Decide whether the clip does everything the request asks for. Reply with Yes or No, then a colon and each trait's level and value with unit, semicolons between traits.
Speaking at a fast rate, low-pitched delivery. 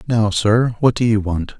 Yes: fast, 225 wpm; low, 110 Hz